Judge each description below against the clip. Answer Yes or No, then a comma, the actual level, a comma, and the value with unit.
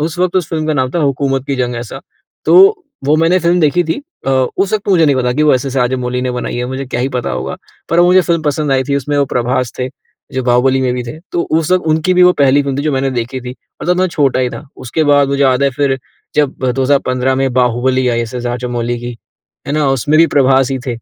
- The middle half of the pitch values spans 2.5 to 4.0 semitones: Yes, average, 3.5 semitones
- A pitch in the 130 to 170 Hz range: Yes, low, 135 Hz